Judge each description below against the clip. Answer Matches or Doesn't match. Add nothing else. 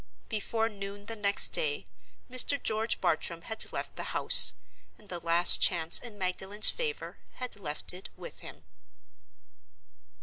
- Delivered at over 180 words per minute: Doesn't match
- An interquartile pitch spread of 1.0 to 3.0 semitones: Doesn't match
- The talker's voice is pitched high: Matches